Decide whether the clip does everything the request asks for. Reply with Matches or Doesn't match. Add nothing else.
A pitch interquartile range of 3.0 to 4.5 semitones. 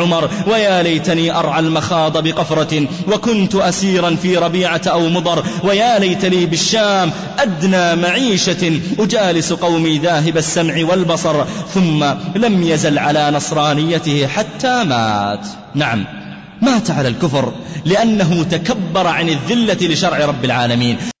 Matches